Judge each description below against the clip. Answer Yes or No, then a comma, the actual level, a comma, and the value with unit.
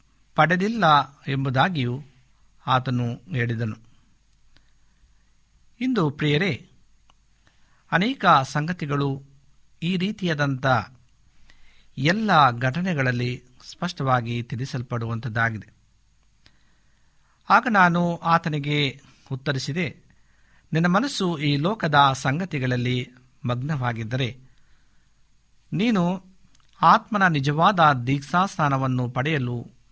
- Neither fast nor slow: No, slow, 60 wpm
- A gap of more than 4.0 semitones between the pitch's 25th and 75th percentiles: Yes, average, 5.1 semitones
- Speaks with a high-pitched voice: No, medium, 140 Hz